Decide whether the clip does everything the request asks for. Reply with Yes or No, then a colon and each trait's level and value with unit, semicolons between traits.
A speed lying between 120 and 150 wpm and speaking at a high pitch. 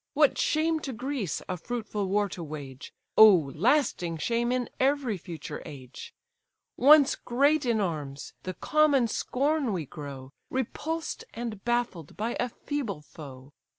Yes: average, 140 wpm; high, 225 Hz